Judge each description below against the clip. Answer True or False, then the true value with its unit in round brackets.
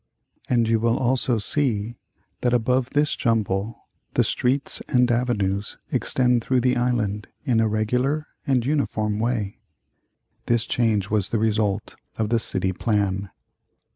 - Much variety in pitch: False (3.0 semitones)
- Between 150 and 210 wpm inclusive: False (140 wpm)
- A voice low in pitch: True (115 Hz)